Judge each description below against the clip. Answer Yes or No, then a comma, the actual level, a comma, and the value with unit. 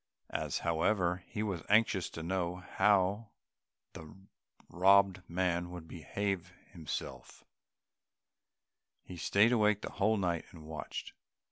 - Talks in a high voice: No, very low, 90 Hz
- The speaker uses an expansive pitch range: No, average, 2.8 semitones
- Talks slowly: Yes, slow, 115 wpm